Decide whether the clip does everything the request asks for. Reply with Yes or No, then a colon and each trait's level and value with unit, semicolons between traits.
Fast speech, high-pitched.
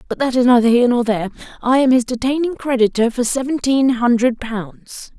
No: average, 185 wpm; high, 245 Hz